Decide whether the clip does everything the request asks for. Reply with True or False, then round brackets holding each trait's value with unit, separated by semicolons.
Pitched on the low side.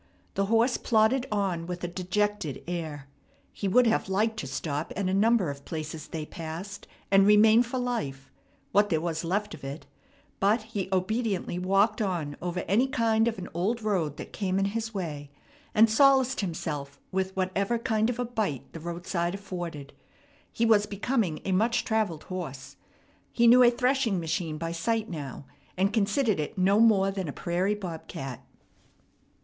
False (195 Hz)